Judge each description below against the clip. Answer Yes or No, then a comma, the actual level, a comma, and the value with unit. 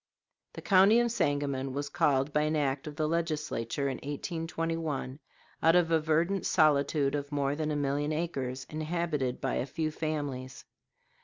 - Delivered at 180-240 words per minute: No, average, 160 wpm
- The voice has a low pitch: No, medium, 150 Hz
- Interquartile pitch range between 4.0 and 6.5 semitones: No, average, 2.8 semitones